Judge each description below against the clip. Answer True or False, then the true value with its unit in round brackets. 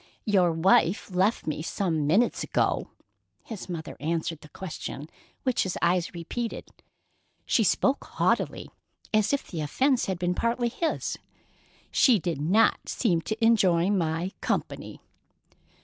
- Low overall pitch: False (185 Hz)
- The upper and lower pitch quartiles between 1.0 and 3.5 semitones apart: False (5.3 semitones)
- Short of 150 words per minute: True (135 wpm)